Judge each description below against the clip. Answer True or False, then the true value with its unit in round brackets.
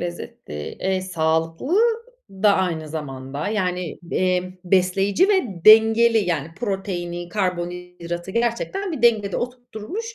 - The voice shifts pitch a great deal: False (4.3 semitones)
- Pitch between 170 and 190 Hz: True (185 Hz)